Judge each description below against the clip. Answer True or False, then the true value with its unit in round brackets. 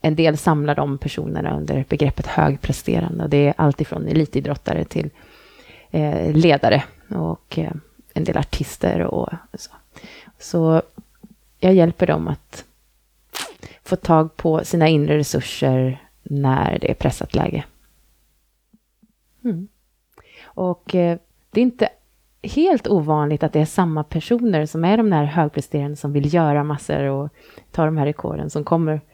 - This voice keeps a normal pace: True (140 wpm)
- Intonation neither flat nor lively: True (3.4 semitones)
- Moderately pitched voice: True (155 Hz)